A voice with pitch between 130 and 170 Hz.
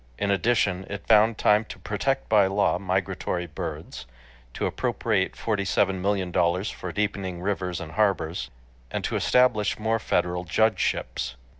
No: low, 100 Hz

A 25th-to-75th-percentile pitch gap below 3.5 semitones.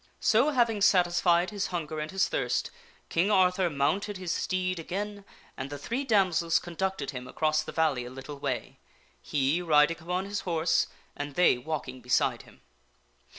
No: average, 4.4 semitones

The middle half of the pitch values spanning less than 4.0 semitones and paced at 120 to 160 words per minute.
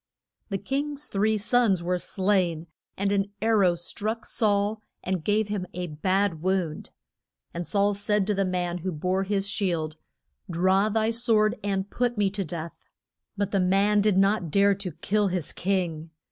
No: narrow, 2.5 semitones; average, 170 wpm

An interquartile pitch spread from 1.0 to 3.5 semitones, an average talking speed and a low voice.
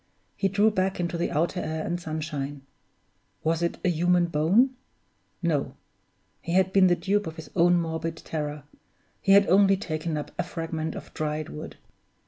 No: average, 3.0 semitones; average, 170 wpm; medium, 170 Hz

